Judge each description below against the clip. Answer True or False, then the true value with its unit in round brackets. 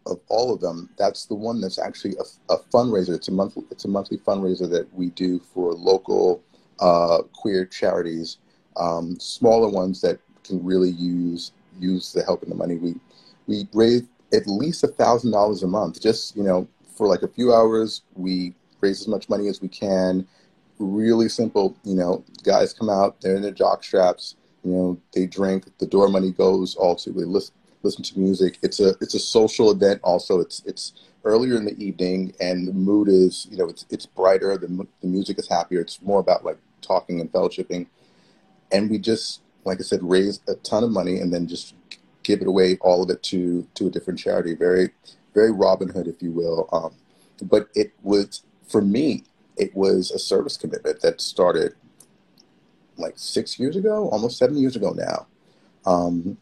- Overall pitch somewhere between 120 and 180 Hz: False (95 Hz)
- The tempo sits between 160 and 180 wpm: False (195 wpm)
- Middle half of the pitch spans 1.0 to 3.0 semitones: True (2.7 semitones)